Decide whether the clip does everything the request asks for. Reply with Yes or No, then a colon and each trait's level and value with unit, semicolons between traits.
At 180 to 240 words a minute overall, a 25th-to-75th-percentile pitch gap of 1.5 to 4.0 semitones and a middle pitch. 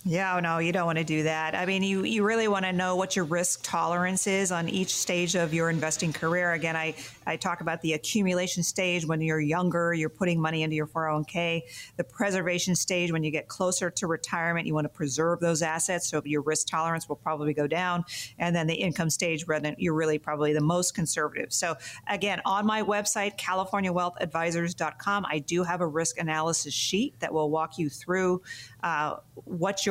Yes: average, 200 wpm; narrow, 2.4 semitones; medium, 170 Hz